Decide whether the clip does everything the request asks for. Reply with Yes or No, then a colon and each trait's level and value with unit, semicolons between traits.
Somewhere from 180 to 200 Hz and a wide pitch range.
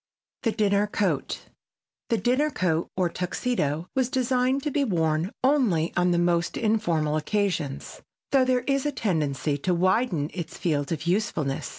Yes: medium, 185 Hz; wide, 7.6 semitones